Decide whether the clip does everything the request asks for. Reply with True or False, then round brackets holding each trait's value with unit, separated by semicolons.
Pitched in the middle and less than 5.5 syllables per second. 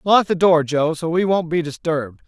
True (165 Hz; 5.2 syllables/s)